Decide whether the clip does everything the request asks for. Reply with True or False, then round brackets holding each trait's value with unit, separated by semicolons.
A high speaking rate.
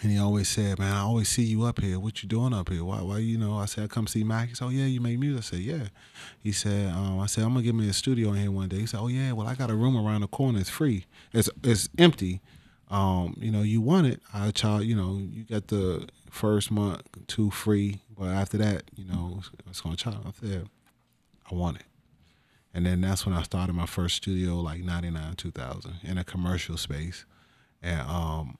True (250 wpm)